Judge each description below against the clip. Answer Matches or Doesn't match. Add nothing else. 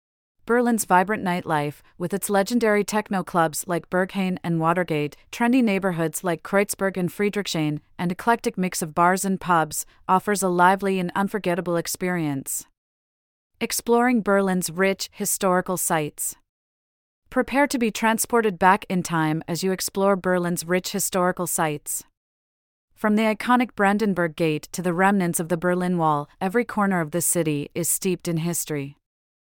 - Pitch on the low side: Doesn't match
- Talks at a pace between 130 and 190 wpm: Matches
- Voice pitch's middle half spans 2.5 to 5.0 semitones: Matches